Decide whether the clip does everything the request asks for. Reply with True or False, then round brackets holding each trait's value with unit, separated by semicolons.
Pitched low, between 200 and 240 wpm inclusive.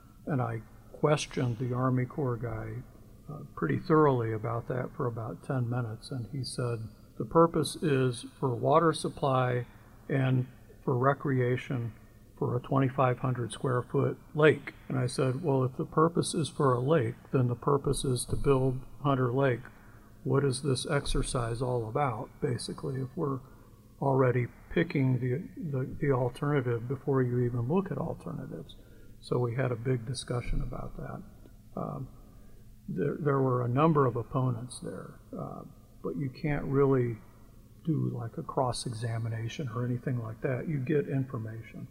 False (130 Hz; 155 wpm)